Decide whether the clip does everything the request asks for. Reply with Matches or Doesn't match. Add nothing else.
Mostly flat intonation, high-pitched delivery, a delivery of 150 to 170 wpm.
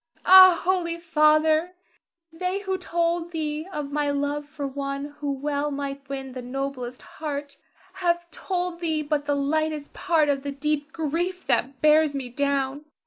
Doesn't match